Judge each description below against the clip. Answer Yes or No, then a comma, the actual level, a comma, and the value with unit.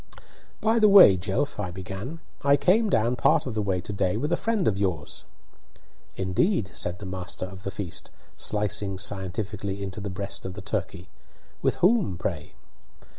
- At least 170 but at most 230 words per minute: Yes, average, 175 wpm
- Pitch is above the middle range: No, low, 100 Hz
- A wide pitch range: Yes, wide, 7.0 semitones